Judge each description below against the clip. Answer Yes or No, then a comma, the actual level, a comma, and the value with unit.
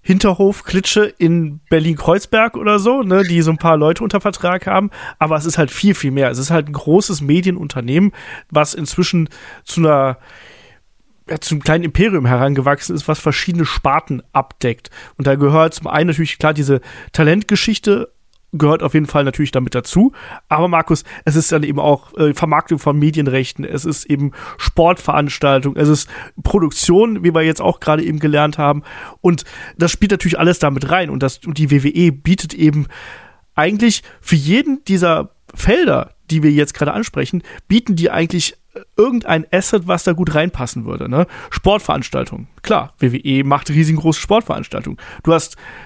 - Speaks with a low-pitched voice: No, medium, 160 Hz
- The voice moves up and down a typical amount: Yes, average, 3.5 semitones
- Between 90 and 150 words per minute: No, average, 165 wpm